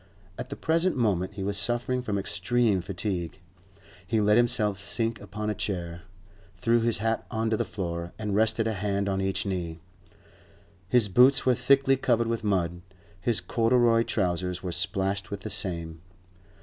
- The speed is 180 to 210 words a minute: No, average, 165 wpm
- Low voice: Yes, low, 105 Hz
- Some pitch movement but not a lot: Yes, average, 3.7 semitones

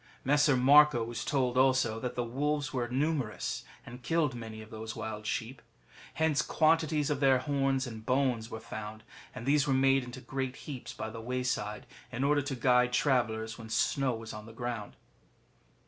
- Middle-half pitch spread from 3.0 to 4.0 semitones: Yes, average, 3.5 semitones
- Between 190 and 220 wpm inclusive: No, average, 180 wpm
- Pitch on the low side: Yes, low, 125 Hz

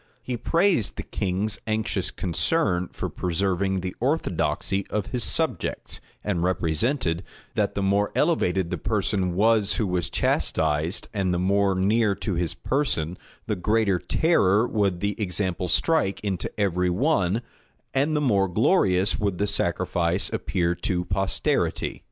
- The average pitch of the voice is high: No, very low, 95 Hz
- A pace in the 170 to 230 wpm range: No, average, 140 wpm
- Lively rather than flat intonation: No, average, 3.5 semitones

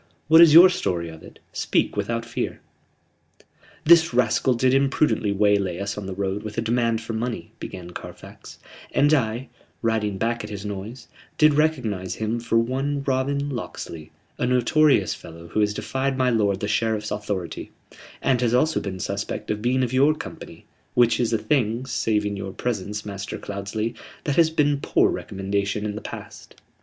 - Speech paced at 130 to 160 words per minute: No, average, 170 wpm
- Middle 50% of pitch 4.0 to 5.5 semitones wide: Yes, average, 4.3 semitones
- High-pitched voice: No, low, 115 Hz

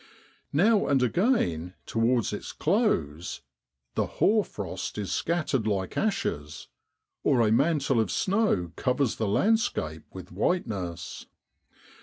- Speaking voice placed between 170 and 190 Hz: No, low, 115 Hz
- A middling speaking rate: No, slow, 120 wpm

